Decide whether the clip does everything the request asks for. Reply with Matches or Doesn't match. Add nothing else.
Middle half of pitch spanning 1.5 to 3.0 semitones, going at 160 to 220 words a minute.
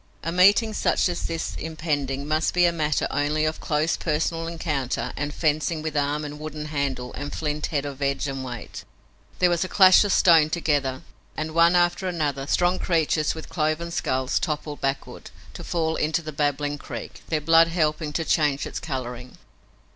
Matches